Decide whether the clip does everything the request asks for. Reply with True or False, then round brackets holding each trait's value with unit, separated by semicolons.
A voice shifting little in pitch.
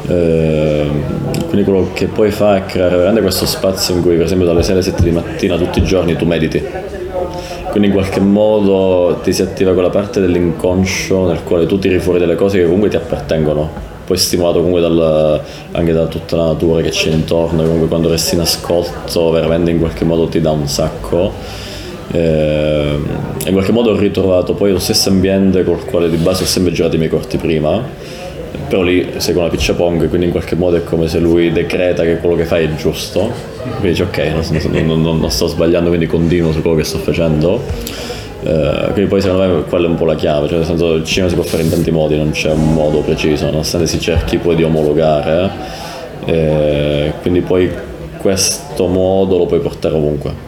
True (2.3 semitones)